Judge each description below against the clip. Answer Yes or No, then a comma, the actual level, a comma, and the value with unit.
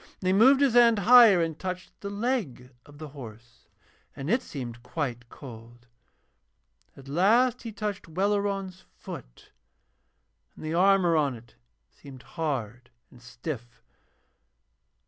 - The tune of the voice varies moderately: No, wide, 8.4 semitones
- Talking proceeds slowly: Yes, slow, 130 wpm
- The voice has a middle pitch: Yes, medium, 160 Hz